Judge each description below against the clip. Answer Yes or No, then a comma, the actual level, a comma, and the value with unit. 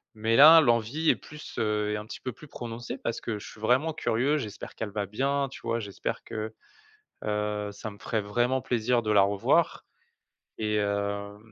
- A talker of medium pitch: No, low, 110 Hz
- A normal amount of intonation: Yes, average, 3.0 semitones